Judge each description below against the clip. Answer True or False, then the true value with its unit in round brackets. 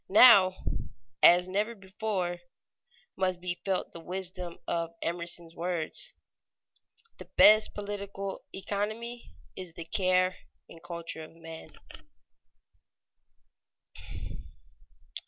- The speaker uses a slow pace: True (90 wpm)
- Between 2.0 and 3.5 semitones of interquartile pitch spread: True (2.8 semitones)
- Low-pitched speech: False (185 Hz)